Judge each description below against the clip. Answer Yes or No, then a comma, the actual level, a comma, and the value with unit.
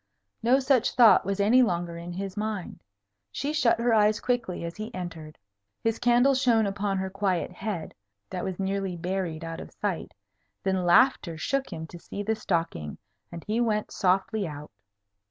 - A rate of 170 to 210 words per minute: Yes, average, 175 wpm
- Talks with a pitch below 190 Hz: No, high, 195 Hz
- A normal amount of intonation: Yes, average, 4.3 semitones